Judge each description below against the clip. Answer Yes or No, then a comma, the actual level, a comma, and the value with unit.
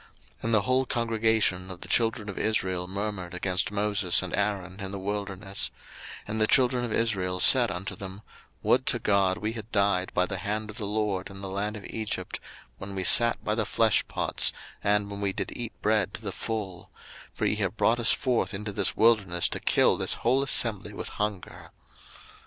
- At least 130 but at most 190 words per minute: No, fast, 205 wpm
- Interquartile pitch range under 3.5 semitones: Yes, narrow, 2.5 semitones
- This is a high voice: No, low, 105 Hz